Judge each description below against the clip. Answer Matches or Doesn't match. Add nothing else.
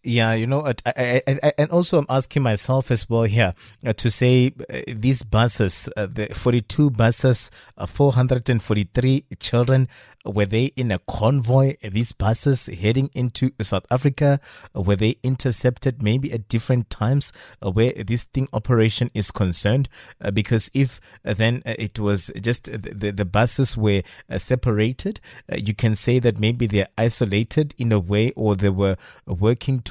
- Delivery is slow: Doesn't match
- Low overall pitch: Matches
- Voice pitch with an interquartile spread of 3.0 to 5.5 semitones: Matches